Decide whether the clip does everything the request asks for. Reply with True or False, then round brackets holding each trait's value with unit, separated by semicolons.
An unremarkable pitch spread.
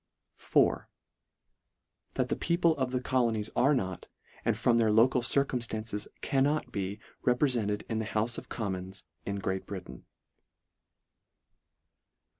True (3.9 semitones)